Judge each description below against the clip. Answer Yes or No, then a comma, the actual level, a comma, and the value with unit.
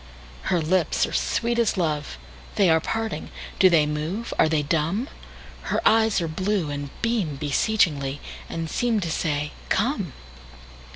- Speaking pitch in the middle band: Yes, medium, 165 Hz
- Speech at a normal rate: No, slow, 120 wpm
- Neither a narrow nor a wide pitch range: No, wide, 5.7 semitones